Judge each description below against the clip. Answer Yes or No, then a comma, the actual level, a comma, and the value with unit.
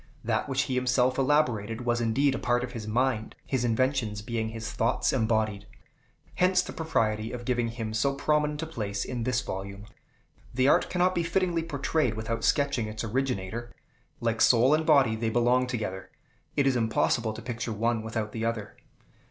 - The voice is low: Yes, low, 120 Hz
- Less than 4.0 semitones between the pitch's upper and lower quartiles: Yes, average, 3.4 semitones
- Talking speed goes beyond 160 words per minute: Yes, average, 175 wpm